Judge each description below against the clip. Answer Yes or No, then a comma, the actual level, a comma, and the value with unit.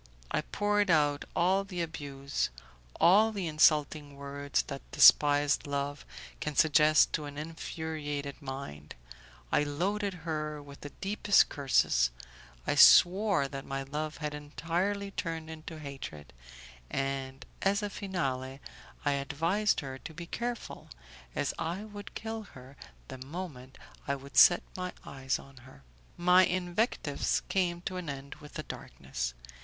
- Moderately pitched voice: Yes, medium, 150 Hz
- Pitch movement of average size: Yes, average, 4.4 semitones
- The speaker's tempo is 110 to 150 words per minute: Yes, average, 140 wpm